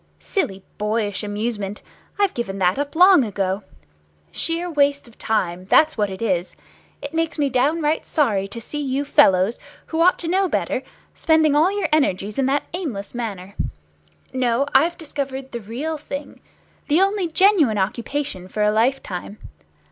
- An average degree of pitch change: No, wide, 7.3 semitones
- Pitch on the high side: Yes, very high, 265 Hz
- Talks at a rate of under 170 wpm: Yes, average, 160 wpm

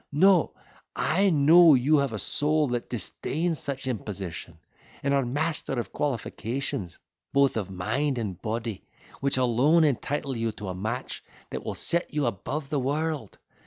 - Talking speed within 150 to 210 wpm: Yes, average, 155 wpm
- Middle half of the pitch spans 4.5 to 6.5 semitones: Yes, average, 4.9 semitones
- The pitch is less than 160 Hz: Yes, low, 135 Hz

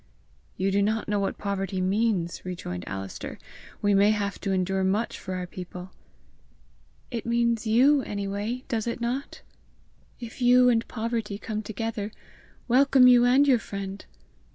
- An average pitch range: Yes, average, 3.4 semitones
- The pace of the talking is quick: No, average, 155 wpm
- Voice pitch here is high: Yes, high, 210 Hz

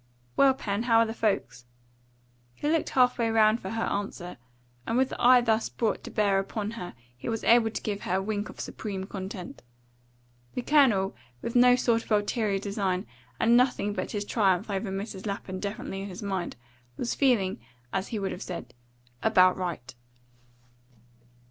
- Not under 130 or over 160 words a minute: No, average, 180 wpm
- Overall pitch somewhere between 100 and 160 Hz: No, high, 205 Hz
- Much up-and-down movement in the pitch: No, average, 3.1 semitones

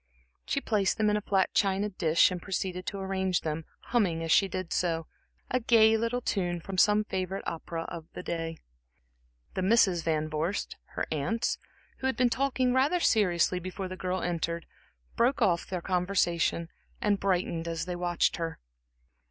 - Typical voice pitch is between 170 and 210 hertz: Yes, medium, 185 Hz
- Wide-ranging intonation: No, average, 3.7 semitones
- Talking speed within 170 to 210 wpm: Yes, average, 175 wpm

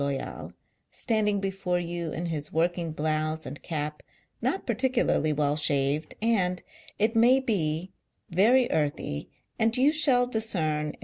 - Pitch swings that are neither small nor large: No, wide, 6.6 semitones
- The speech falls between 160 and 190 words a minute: No, average, 140 wpm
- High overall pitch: No, medium, 175 Hz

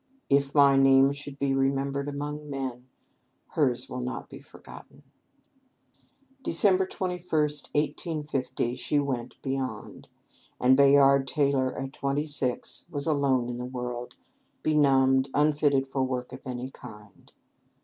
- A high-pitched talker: No, low, 135 Hz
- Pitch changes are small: Yes, narrow, 1.9 semitones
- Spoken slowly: Yes, slow, 125 wpm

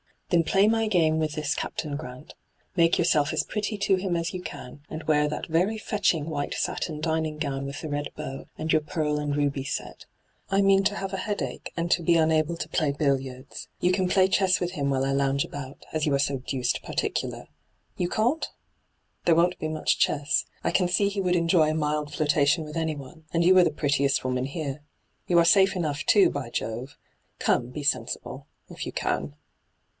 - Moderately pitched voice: Yes, medium, 155 Hz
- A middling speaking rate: No, fast, 210 wpm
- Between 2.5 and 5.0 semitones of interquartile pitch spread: Yes, average, 3.8 semitones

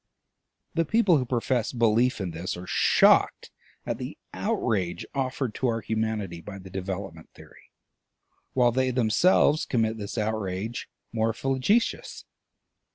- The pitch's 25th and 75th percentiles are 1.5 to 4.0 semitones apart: No, average, 4.6 semitones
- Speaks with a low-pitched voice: Yes, low, 110 Hz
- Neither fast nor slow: No, slow, 130 wpm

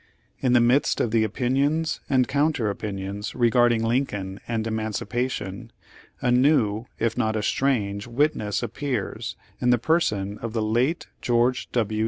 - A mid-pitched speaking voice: No, low, 120 Hz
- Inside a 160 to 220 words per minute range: No, average, 150 wpm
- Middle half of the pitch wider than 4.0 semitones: No, average, 3.0 semitones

